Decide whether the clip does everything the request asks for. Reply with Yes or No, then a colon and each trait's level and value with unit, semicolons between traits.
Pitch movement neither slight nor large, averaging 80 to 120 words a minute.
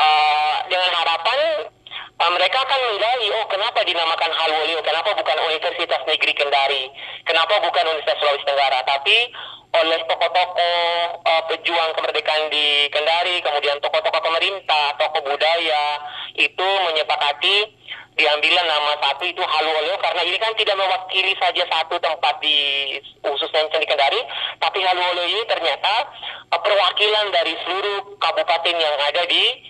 No: average, 3.2 semitones; average, 130 wpm